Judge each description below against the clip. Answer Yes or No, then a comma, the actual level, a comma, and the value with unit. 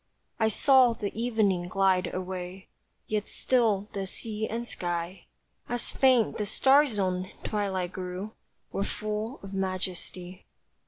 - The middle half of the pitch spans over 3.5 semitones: No, average, 3.2 semitones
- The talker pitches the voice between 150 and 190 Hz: No, high, 200 Hz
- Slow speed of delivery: Yes, slow, 125 wpm